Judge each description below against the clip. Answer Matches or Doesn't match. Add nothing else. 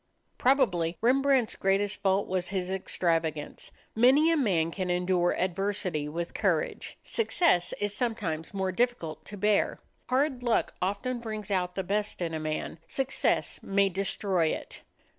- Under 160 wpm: Matches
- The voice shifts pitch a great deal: Doesn't match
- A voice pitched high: Matches